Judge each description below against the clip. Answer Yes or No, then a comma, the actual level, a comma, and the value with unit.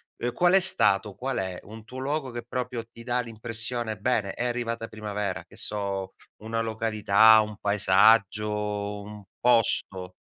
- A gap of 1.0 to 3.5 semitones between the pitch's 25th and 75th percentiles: Yes, narrow, 2.6 semitones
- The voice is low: Yes, low, 110 Hz